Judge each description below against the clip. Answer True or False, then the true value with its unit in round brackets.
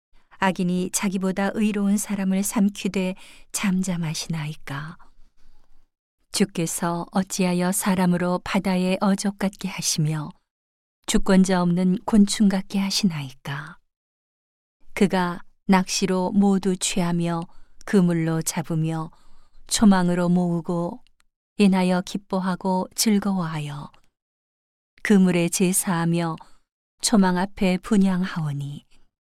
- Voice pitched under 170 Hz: False (185 Hz)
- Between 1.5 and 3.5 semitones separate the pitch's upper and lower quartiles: True (2.5 semitones)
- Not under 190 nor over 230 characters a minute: True (225 characters per minute)